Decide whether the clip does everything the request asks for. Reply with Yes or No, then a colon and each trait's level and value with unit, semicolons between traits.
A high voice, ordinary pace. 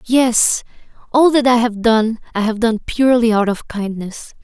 Yes: high, 230 Hz; average, 175 wpm